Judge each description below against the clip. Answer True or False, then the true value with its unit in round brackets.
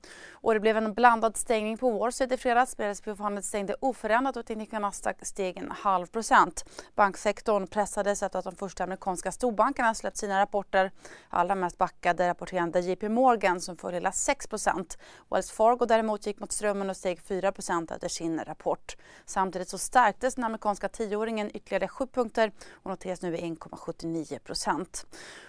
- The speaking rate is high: False (150 wpm)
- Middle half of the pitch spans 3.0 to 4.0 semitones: True (3.3 semitones)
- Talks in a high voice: True (205 Hz)